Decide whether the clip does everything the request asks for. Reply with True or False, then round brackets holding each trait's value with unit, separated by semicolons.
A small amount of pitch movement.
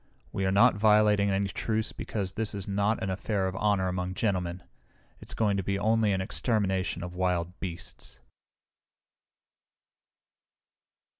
True (2.2 semitones)